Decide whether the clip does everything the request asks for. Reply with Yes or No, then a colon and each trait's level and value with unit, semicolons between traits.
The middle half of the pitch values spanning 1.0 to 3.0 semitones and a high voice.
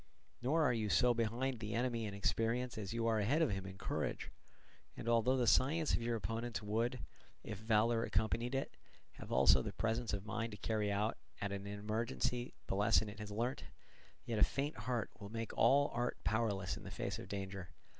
No: average, 2.7 semitones; low, 115 Hz